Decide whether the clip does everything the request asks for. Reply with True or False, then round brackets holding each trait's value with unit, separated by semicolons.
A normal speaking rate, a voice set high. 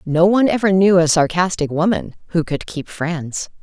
False (180 wpm; 175 Hz)